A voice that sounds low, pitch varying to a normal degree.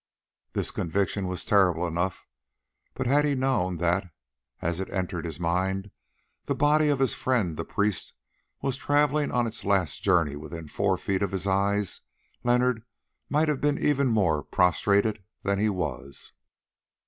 No: low, 100 Hz; wide, 6.0 semitones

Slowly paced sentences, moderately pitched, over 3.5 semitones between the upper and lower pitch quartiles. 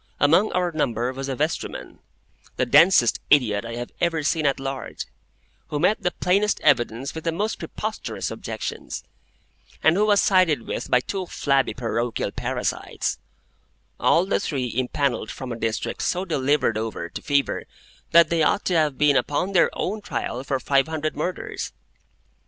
No: average, 160 wpm; medium, 145 Hz; average, 5.1 semitones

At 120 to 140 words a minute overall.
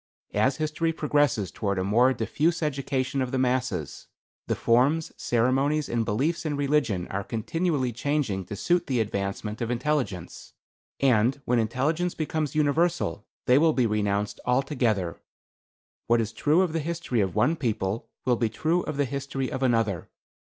No: average, 160 wpm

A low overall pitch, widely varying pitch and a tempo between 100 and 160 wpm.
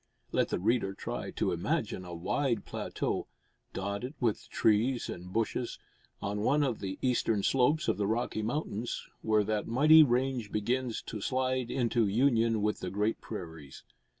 No: low, 115 Hz; average, 3.8 semitones; average, 155 wpm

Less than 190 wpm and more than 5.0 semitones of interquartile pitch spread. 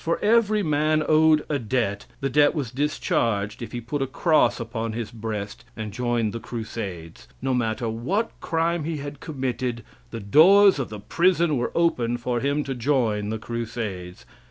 Yes: average, 175 wpm; wide, 5.4 semitones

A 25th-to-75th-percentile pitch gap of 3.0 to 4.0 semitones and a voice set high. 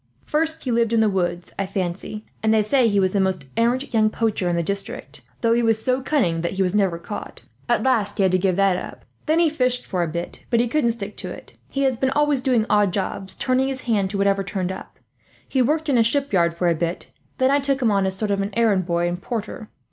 No: average, 5.0 semitones; high, 215 Hz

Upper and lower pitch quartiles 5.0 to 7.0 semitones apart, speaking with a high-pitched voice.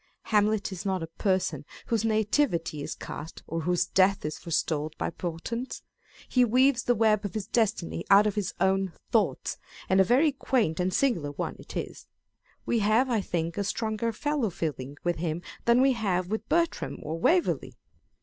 Yes: average, 5.3 semitones; high, 200 Hz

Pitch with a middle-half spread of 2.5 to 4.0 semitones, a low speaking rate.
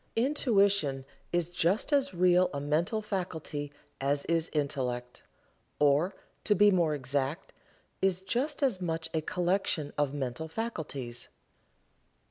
No: average, 5.1 semitones; slow, 120 wpm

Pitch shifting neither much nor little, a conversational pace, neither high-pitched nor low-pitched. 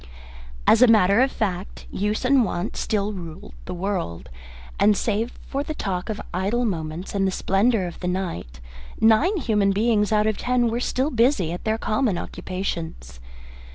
No: average, 4.1 semitones; average, 170 wpm; high, 205 Hz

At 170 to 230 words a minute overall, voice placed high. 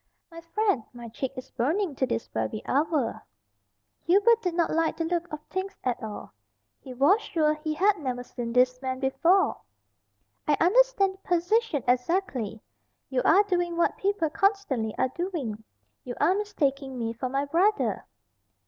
No: average, 160 wpm; very high, 310 Hz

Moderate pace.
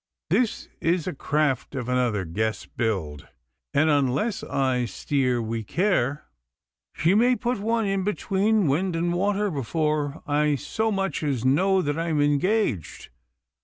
Yes: average, 145 wpm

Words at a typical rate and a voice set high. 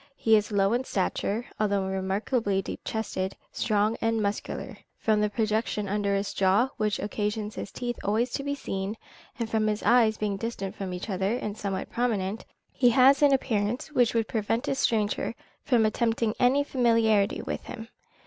Yes: average, 175 wpm; high, 215 Hz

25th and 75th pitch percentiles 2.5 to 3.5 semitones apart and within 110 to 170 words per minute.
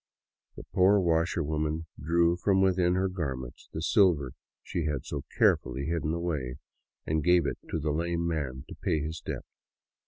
Yes: average, 2.9 semitones; average, 160 wpm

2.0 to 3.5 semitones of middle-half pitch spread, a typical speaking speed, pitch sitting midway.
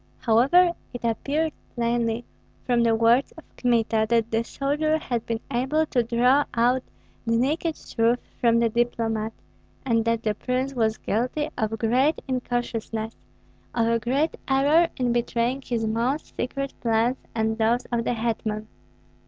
No: narrow, 2.5 semitones; average, 150 wpm; high, 235 Hz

